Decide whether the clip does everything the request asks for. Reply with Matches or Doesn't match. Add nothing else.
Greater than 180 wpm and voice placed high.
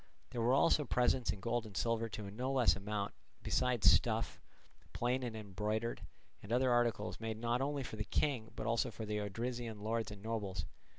Doesn't match